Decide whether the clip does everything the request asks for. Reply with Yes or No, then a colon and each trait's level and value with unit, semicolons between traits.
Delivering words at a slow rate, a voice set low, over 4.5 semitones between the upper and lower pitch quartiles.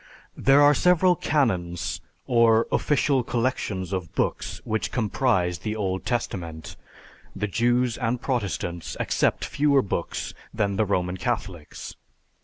Yes: slow, 120 wpm; low, 110 Hz; wide, 5.4 semitones